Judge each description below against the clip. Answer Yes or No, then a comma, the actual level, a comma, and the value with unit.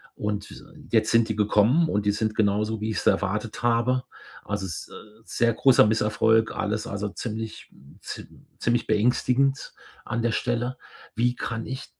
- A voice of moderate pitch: No, low, 110 Hz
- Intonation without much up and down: Yes, narrow, 2.2 semitones